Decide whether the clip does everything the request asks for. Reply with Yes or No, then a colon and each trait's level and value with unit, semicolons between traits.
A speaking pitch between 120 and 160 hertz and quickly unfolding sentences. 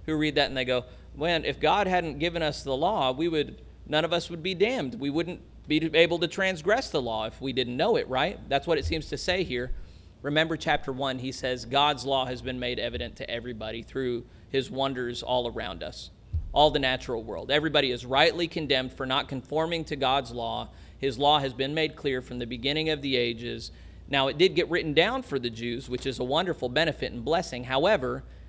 Yes: low, 135 Hz; fast, 225 wpm